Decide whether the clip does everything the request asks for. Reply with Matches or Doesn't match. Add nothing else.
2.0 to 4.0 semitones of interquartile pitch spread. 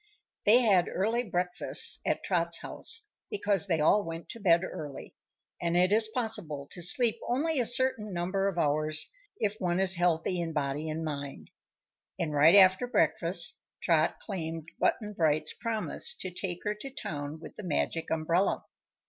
Doesn't match